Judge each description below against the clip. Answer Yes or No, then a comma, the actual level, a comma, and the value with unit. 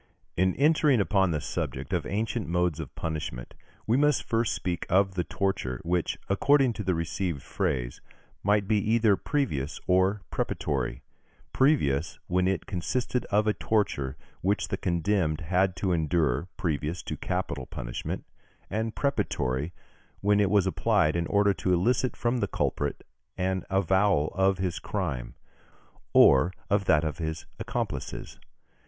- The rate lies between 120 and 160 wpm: Yes, average, 145 wpm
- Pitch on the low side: Yes, very low, 95 Hz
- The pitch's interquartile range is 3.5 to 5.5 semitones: Yes, average, 4.6 semitones